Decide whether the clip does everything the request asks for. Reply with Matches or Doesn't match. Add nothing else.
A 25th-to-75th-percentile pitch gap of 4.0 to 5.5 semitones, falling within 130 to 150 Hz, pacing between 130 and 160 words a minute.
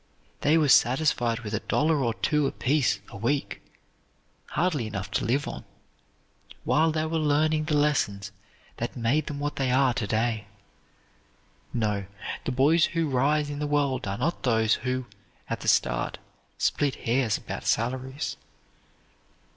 Matches